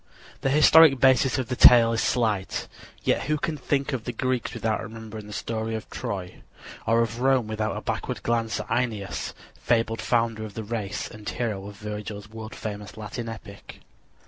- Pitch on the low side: Yes, low, 115 Hz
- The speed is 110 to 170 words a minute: No, average, 180 wpm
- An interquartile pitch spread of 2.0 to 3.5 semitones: Yes, narrow, 2.4 semitones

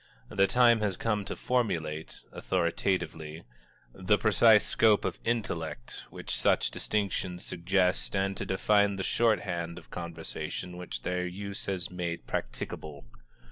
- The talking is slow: Yes, slow, 130 wpm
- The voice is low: Yes, very low, 95 Hz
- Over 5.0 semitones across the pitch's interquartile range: No, average, 3.3 semitones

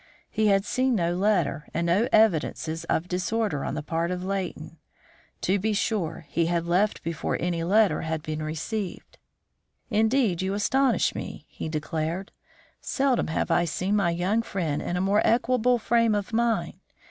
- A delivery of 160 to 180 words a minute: Yes, average, 165 wpm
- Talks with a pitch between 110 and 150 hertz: No, medium, 185 Hz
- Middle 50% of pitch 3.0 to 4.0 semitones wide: No, average, 4.6 semitones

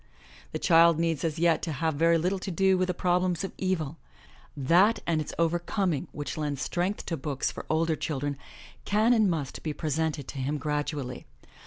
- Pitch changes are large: No, average, 3.4 semitones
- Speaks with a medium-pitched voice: Yes, medium, 165 Hz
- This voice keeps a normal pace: Yes, average, 190 wpm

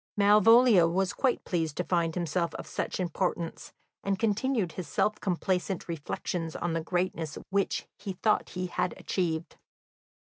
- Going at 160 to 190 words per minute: No, average, 145 wpm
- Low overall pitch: No, medium, 180 Hz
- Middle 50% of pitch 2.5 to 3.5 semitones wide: Yes, average, 3.1 semitones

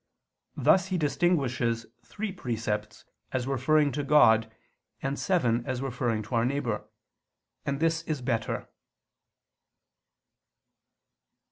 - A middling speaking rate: No, slow, 105 wpm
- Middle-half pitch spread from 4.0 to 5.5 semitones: Yes, average, 4.6 semitones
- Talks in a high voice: No, low, 135 Hz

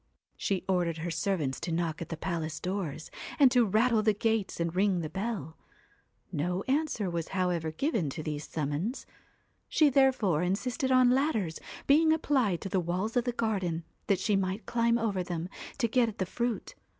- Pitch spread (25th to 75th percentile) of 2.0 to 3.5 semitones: No, wide, 5.6 semitones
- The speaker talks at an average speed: Yes, average, 180 wpm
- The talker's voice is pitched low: No, high, 195 Hz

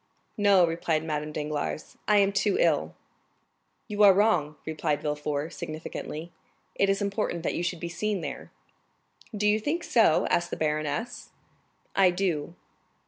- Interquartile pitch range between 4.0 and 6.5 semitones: Yes, average, 4.8 semitones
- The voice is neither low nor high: Yes, medium, 175 Hz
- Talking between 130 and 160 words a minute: Yes, average, 145 wpm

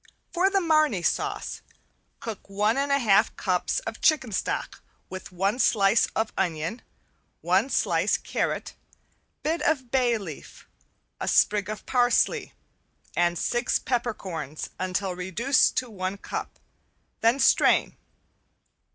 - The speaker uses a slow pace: Yes, slow, 125 wpm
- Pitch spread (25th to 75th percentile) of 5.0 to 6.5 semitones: Yes, wide, 5.4 semitones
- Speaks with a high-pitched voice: Yes, high, 215 Hz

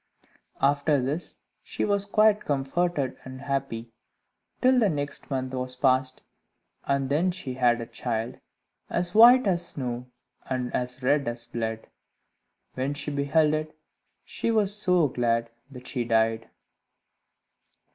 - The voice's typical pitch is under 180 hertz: Yes, low, 135 Hz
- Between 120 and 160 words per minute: Yes, slow, 135 wpm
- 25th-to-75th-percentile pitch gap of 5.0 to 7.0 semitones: Yes, average, 5.3 semitones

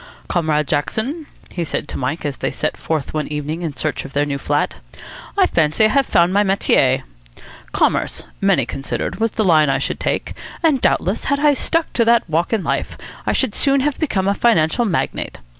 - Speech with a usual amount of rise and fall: No, wide, 7.8 semitones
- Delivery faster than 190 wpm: Yes, average, 200 wpm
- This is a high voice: No, medium, 175 Hz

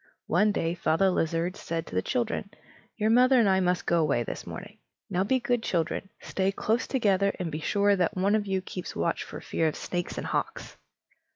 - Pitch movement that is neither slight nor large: Yes, average, 3.7 semitones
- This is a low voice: No, high, 190 Hz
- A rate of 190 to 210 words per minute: Yes, fast, 205 wpm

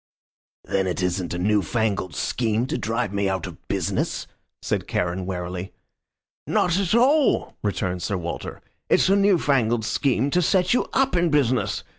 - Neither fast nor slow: Yes, average, 165 wpm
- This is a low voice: Yes, low, 110 Hz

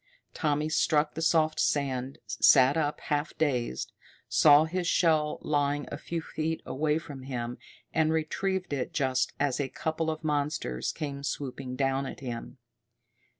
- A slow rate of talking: No, average, 150 wpm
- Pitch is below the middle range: No, medium, 145 Hz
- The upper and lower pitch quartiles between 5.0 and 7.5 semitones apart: No, average, 2.9 semitones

